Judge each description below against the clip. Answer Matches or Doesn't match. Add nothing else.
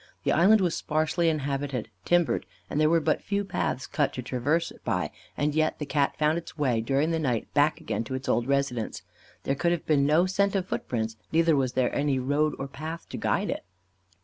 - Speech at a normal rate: Doesn't match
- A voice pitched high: Doesn't match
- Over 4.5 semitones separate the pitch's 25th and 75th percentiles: Doesn't match